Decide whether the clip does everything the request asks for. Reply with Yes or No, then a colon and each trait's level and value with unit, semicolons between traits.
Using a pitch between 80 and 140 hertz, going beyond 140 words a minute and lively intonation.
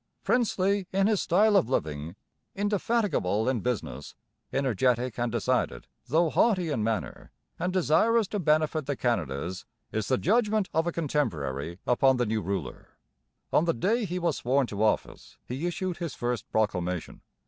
Yes: low, 135 Hz; average, 155 wpm; wide, 9.0 semitones